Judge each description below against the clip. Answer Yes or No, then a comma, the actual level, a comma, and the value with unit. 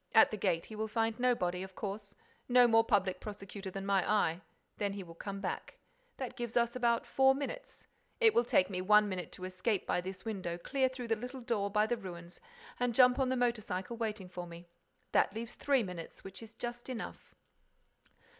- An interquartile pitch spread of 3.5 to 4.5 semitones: Yes, average, 4.2 semitones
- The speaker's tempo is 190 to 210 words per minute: Yes, fast, 205 wpm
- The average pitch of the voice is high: Yes, high, 215 Hz